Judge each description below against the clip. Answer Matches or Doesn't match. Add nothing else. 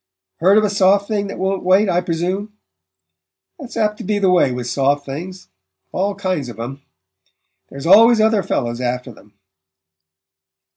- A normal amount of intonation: Doesn't match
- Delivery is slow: Doesn't match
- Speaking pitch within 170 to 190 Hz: Matches